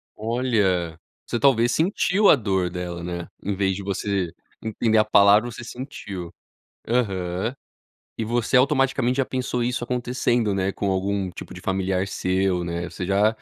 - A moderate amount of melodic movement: Yes, average, 4.5 semitones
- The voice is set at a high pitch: No, low, 100 Hz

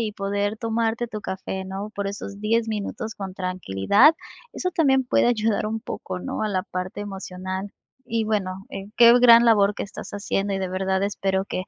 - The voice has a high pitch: Yes, high, 205 Hz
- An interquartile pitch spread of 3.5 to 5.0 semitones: No, average, 2.7 semitones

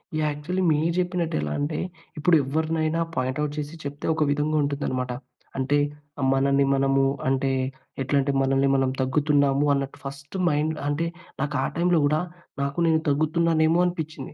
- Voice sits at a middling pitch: Yes, medium, 145 Hz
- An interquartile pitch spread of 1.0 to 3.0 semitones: Yes, narrow, 2.5 semitones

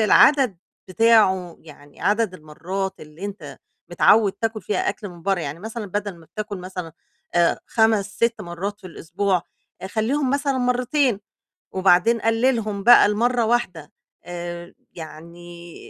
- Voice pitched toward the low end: No, high, 200 Hz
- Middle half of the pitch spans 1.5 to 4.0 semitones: No, average, 4.7 semitones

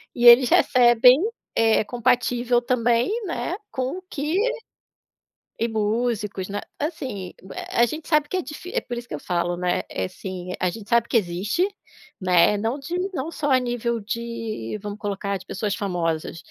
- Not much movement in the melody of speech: No, average, 4.0 semitones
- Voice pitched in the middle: No, high, 230 Hz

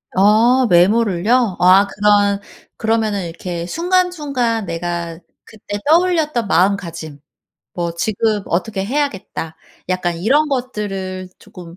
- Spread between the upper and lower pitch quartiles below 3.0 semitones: No, average, 5.2 semitones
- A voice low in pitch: No, high, 205 Hz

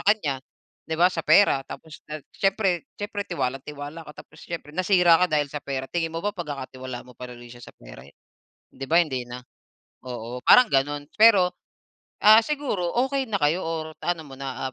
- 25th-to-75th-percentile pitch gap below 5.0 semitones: No, average, 5.3 semitones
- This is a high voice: No, medium, 155 Hz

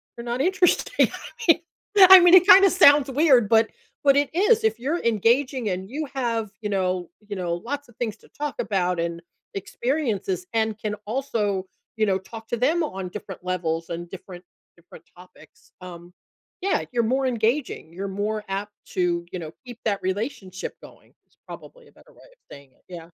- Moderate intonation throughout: No, wide, 7.0 semitones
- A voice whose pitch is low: No, high, 220 Hz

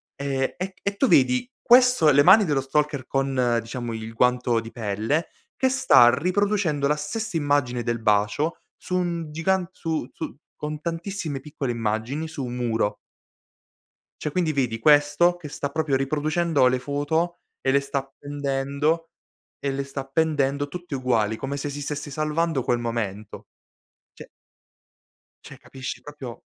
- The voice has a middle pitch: Yes, medium, 145 Hz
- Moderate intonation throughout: Yes, average, 4.2 semitones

